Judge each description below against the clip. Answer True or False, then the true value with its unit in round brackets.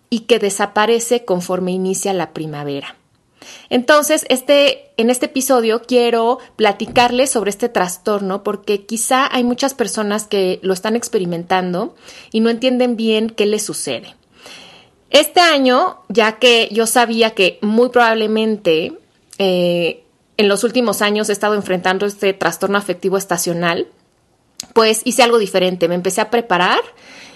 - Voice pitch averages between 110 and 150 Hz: False (220 Hz)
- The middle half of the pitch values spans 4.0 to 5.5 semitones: True (4.3 semitones)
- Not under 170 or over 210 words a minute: False (135 wpm)